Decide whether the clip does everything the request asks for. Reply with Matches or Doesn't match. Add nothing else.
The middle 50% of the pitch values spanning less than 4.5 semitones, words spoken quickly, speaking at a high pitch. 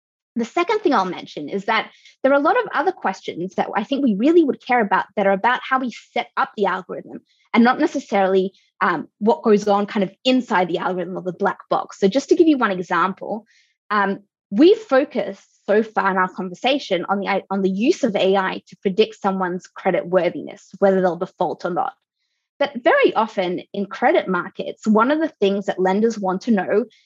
Doesn't match